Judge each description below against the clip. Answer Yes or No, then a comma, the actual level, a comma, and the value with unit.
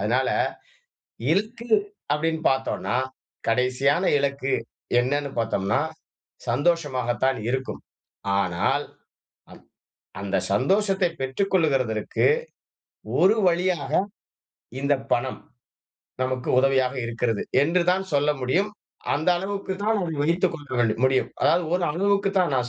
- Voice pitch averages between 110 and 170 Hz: Yes, medium, 140 Hz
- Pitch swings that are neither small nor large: No, wide, 5.8 semitones